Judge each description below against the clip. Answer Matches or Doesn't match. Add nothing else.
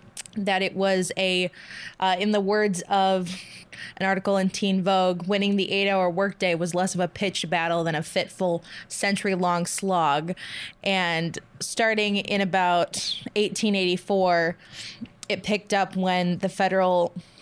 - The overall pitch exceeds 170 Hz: Matches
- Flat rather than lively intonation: Matches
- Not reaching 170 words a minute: Matches